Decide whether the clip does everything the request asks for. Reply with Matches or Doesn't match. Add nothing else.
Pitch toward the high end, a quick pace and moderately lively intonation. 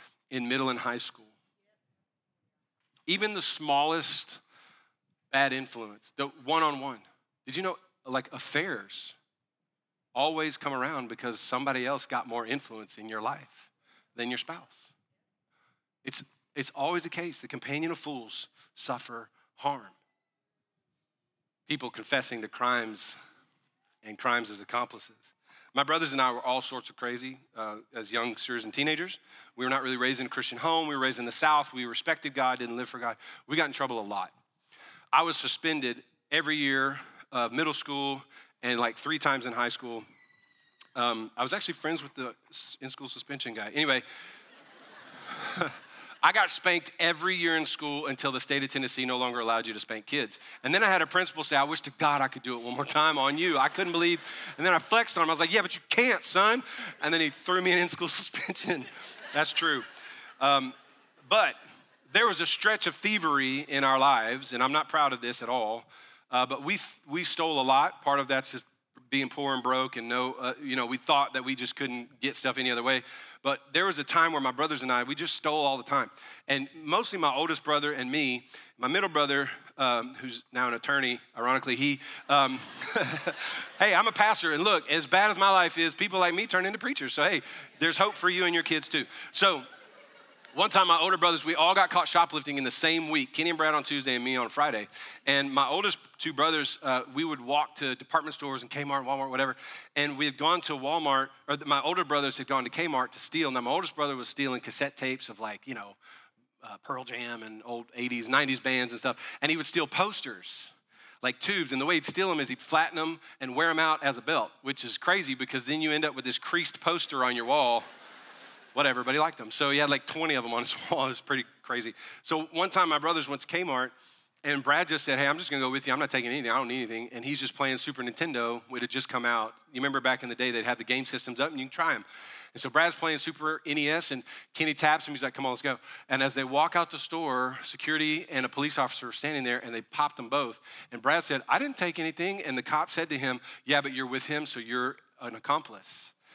Doesn't match